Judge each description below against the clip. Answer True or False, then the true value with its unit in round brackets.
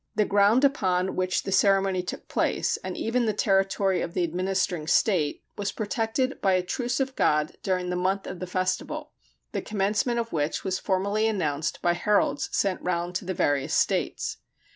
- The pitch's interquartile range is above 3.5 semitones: False (2.7 semitones)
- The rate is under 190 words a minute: True (180 wpm)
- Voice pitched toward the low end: False (190 Hz)